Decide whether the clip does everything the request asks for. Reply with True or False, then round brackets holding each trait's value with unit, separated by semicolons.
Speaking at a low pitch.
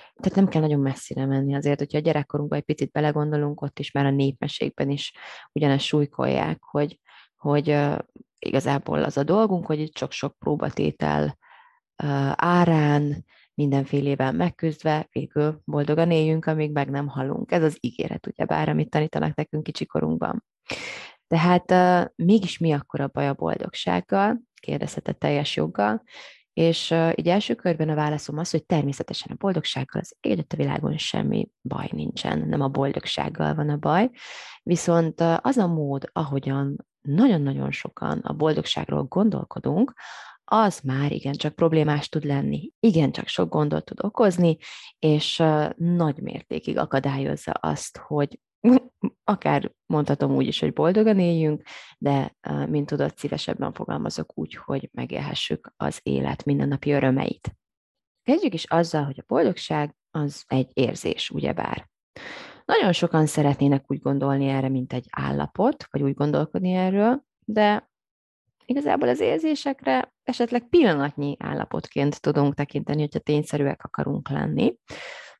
False (150 Hz)